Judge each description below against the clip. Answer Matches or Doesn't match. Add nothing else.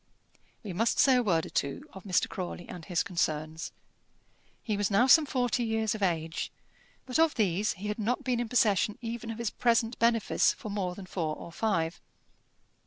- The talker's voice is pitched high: Matches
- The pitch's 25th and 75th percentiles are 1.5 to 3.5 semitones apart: Doesn't match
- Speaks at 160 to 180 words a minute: Doesn't match